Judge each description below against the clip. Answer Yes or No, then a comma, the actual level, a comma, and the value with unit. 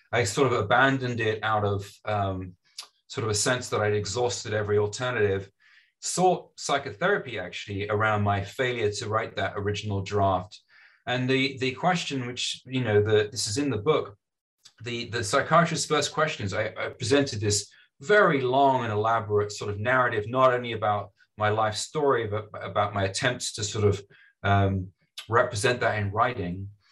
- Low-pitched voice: Yes, low, 110 Hz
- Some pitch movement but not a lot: Yes, average, 3.8 semitones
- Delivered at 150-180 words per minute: Yes, average, 165 wpm